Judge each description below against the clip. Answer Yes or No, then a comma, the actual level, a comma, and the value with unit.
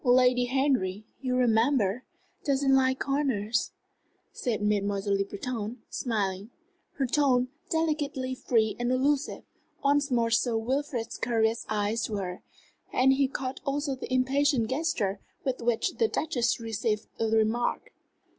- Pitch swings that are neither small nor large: Yes, average, 3.5 semitones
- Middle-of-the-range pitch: No, high, 245 Hz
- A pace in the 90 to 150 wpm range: Yes, slow, 135 wpm